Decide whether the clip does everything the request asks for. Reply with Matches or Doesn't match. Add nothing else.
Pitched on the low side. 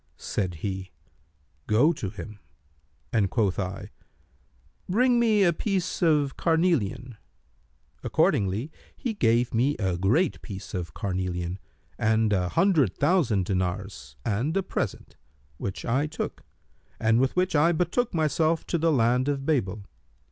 Matches